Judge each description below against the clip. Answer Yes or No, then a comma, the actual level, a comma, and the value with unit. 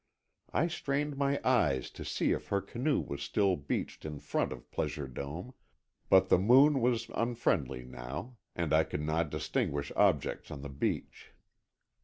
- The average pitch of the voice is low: Yes, very low, 90 Hz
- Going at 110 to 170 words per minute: Yes, average, 160 wpm